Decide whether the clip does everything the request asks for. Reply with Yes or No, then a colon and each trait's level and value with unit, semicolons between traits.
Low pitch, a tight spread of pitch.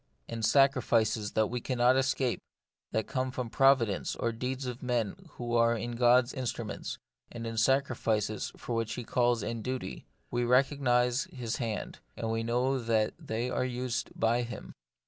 Yes: low, 120 Hz; narrow, 2.0 semitones